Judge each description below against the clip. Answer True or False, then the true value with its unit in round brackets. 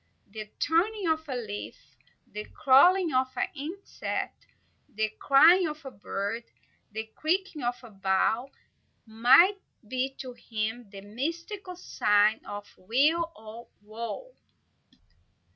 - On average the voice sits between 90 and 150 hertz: False (255 Hz)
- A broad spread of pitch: True (7.0 semitones)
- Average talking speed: False (120 wpm)